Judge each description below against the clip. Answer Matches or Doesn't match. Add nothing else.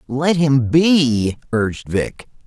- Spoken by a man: Matches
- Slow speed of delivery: Matches